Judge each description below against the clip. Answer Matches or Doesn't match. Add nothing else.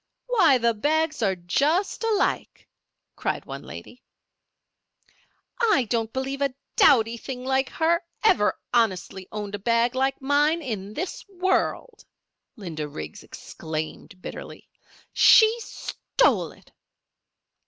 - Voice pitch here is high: Matches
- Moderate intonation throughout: Doesn't match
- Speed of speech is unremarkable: Doesn't match